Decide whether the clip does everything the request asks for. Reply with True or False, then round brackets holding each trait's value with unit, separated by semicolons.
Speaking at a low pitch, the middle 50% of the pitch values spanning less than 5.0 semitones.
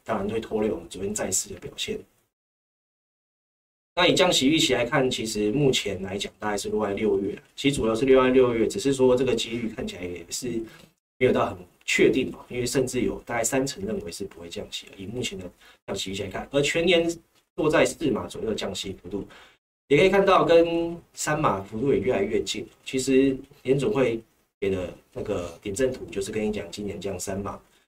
False (120 Hz; 5.4 semitones)